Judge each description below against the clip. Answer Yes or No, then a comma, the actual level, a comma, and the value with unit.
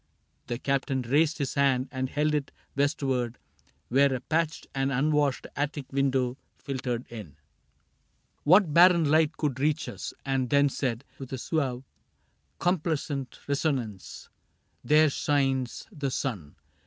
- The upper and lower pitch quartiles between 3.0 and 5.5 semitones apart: No, narrow, 2.6 semitones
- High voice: No, medium, 140 Hz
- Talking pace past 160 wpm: No, average, 145 wpm